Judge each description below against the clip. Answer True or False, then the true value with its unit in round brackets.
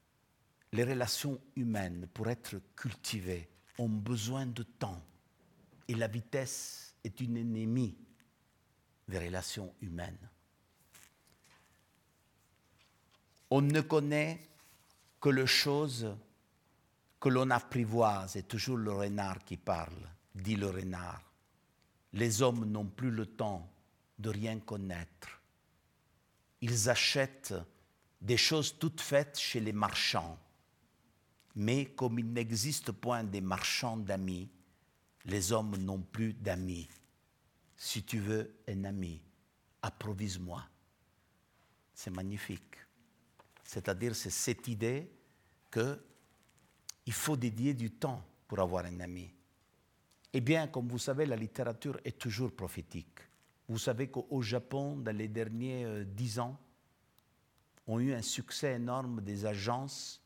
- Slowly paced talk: True (115 wpm)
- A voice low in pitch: True (115 Hz)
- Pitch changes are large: False (4.3 semitones)